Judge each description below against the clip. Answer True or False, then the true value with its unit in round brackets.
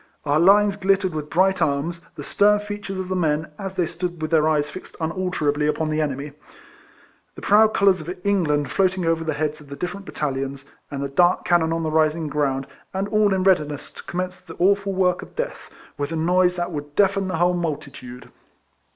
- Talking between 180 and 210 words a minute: True (205 wpm)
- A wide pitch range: False (3.9 semitones)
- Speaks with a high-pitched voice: False (170 Hz)